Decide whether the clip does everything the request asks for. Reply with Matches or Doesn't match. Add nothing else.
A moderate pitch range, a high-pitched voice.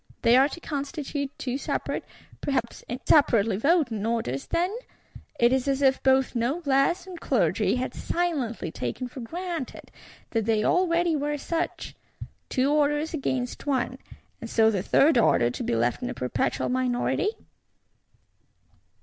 Matches